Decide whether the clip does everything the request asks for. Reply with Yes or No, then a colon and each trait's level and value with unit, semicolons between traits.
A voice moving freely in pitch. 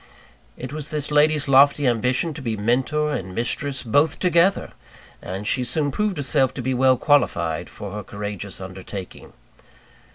Yes: wide, 5.9 semitones